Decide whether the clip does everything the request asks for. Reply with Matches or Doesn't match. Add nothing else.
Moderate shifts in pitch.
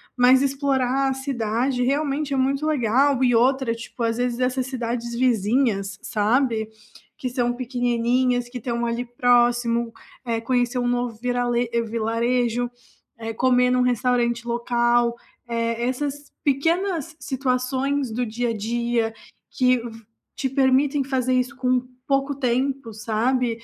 Doesn't match